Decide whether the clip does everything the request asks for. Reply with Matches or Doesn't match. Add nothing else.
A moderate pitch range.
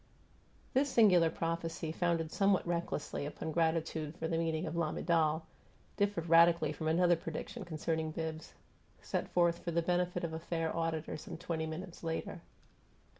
Doesn't match